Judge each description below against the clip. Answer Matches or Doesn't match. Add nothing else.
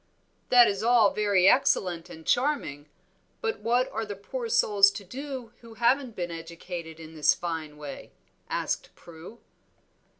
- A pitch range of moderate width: Doesn't match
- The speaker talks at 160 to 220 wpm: Doesn't match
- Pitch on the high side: Matches